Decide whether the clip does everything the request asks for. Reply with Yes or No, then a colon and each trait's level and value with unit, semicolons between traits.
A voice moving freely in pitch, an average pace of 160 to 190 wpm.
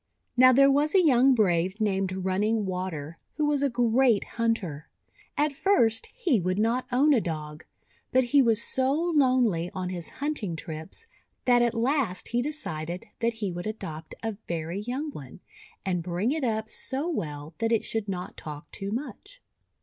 Yes: wide, 6.4 semitones; average, 175 wpm